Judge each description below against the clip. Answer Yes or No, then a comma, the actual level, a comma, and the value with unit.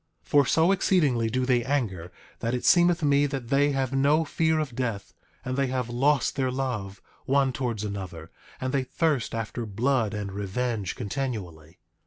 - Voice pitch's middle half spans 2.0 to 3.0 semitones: No, average, 4.5 semitones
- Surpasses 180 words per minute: No, average, 175 wpm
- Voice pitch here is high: No, low, 130 Hz